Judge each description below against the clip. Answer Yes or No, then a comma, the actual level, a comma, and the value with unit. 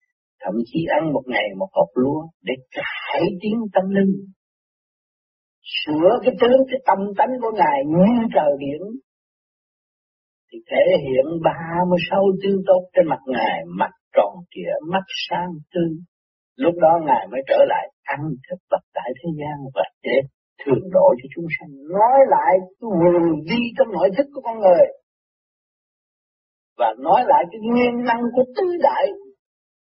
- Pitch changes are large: Yes, wide, 8.0 semitones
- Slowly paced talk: Yes, slow, 160 wpm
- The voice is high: Yes, high, 195 Hz